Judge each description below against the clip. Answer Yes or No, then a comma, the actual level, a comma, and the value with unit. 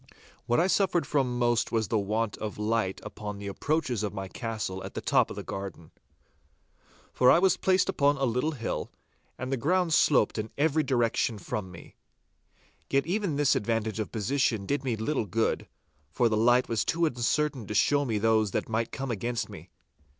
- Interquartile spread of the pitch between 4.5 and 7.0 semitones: Yes, average, 4.8 semitones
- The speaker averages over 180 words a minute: Yes, average, 190 wpm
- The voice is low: Yes, low, 115 Hz